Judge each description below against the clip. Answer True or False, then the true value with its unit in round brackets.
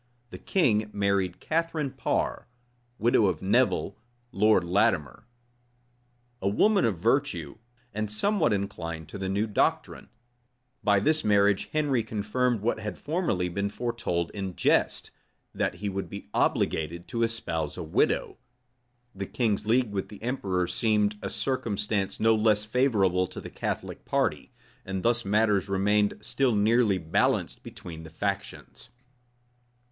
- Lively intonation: False (3.3 semitones)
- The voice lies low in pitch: True (105 Hz)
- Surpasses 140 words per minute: False (135 wpm)